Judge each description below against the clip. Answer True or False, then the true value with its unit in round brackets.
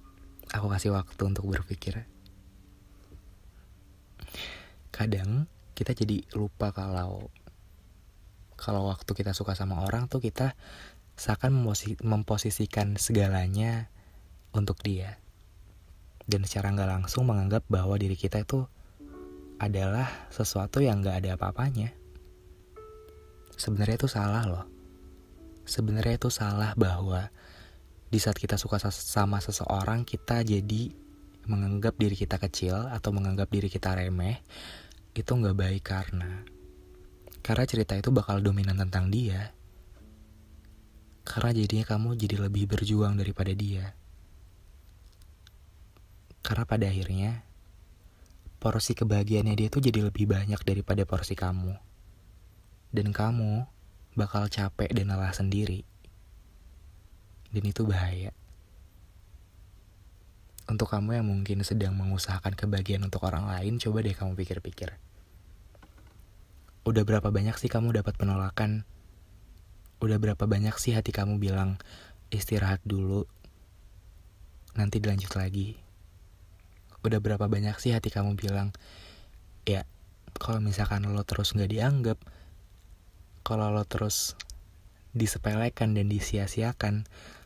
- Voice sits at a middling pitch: False (100 Hz)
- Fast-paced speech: False (110 wpm)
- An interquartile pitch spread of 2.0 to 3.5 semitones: True (2.4 semitones)